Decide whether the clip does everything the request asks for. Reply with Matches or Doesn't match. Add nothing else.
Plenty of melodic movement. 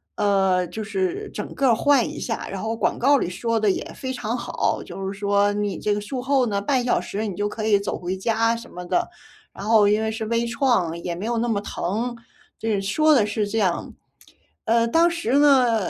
Doesn't match